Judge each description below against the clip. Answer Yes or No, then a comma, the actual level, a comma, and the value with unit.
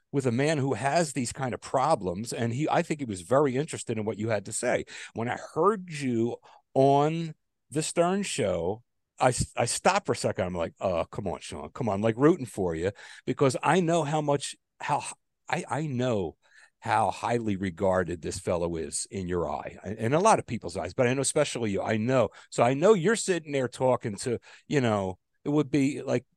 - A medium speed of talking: No, fast, 215 wpm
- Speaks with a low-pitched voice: Yes, low, 130 Hz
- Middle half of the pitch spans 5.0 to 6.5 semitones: Yes, wide, 5.6 semitones